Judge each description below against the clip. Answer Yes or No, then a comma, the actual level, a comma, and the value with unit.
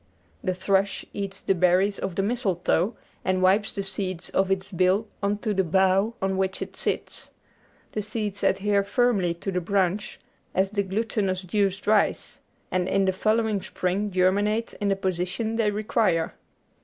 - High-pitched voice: Yes, high, 195 Hz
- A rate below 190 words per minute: Yes, average, 165 wpm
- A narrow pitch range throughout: Yes, narrow, 1.9 semitones